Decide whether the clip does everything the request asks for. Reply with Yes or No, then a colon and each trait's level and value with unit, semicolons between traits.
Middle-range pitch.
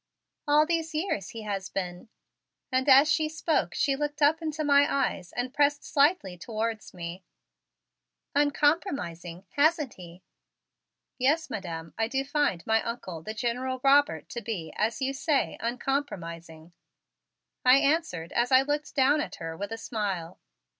No: very high, 255 Hz